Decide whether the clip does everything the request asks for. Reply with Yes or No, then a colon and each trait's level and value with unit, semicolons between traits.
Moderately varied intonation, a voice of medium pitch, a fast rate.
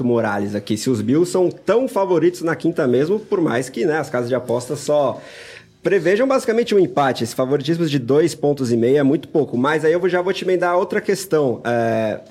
No: wide, 6.9 semitones; medium, 155 Hz; fast, 215 wpm